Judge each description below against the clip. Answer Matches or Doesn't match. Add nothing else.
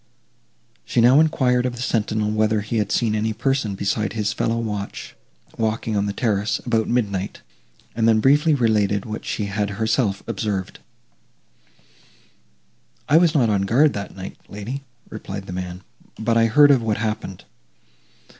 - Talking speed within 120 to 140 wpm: Doesn't match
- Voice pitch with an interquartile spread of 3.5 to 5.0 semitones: Doesn't match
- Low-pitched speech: Matches